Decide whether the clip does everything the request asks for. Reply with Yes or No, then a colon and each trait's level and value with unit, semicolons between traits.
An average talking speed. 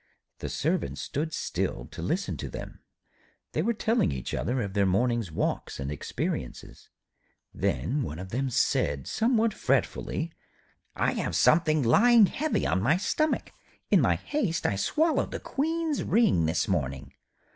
Yes: average, 150 wpm